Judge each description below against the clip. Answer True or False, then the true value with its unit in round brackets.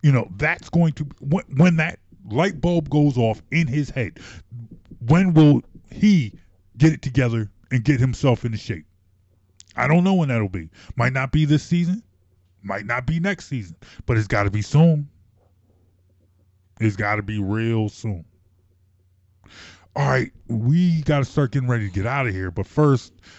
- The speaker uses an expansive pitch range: True (7.6 semitones)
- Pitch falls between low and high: False (115 Hz)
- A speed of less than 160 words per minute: False (175 wpm)